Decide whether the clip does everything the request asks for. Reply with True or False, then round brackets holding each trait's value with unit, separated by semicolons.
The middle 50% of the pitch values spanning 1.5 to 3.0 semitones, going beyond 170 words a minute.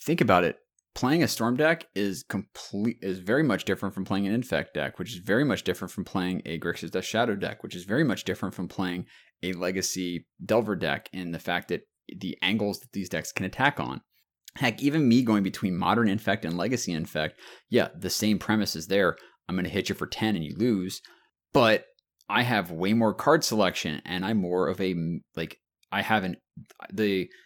True (2.7 semitones; 205 wpm)